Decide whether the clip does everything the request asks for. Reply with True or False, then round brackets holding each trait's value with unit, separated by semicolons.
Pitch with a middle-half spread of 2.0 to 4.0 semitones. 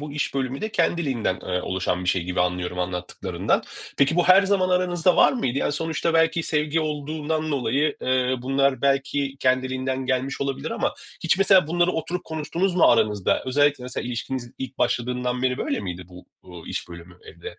False (4.9 semitones)